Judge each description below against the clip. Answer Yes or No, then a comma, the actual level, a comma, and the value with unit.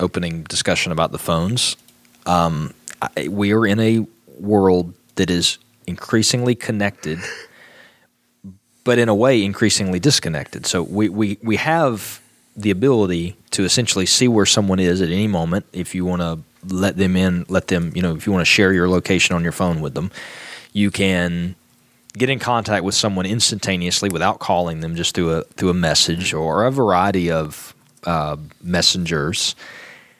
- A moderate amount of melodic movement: Yes, average, 3.5 semitones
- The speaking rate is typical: Yes, average, 165 wpm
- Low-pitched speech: Yes, very low, 95 Hz